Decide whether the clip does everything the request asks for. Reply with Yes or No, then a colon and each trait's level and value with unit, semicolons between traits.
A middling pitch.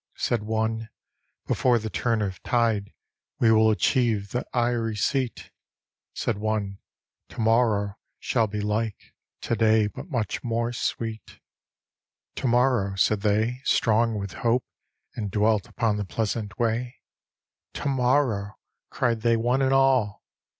No: low, 115 Hz